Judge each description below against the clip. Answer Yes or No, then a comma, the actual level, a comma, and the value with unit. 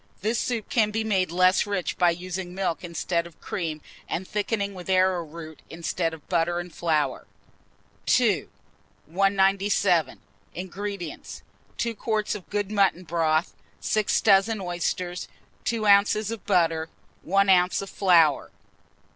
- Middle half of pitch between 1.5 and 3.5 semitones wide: Yes, average, 3.0 semitones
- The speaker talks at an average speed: No, slow, 130 wpm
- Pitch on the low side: No, medium, 185 Hz